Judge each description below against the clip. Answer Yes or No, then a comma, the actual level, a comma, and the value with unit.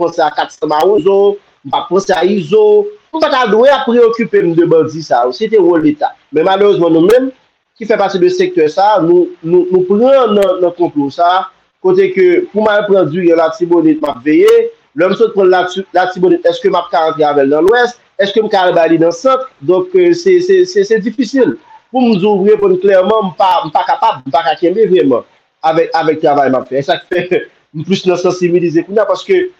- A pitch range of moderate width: No, wide, 8.0 semitones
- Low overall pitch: No, high, 200 Hz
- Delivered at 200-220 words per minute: Yes, average, 215 wpm